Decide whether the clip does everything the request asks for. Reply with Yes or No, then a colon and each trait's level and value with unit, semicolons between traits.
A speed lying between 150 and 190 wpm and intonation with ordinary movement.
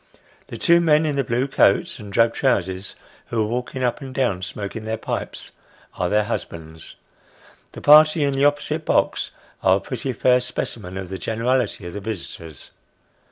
No: average, 175 wpm; wide, 5.8 semitones